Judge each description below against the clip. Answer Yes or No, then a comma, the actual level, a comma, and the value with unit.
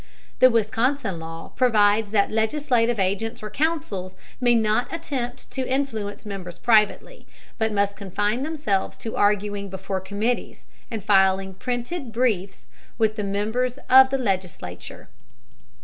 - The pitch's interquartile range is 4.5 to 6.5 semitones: No, average, 3.8 semitones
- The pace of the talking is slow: Yes, slow, 130 wpm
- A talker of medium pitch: No, high, 220 Hz